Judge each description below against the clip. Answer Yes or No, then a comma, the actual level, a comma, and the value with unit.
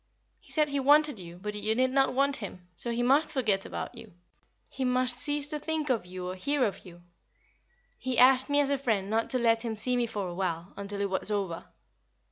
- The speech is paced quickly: Yes, fast, 230 wpm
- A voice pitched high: Yes, high, 235 Hz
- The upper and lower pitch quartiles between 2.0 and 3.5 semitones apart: No, wide, 5.4 semitones